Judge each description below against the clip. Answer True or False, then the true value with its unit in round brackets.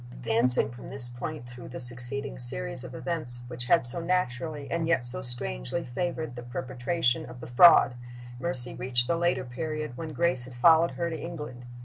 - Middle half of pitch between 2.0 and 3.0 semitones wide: False (4.9 semitones)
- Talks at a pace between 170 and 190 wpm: True (180 wpm)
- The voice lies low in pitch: True (125 Hz)